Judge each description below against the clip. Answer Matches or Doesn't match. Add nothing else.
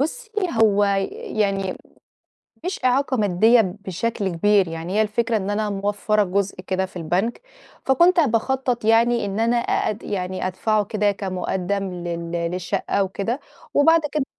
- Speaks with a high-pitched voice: Matches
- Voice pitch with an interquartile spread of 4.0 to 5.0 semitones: Doesn't match